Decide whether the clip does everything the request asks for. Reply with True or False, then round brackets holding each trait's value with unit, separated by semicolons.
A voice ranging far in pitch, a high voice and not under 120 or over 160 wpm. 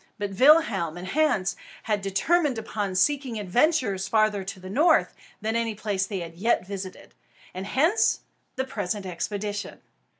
False (4.9 semitones; 205 Hz; 145 wpm)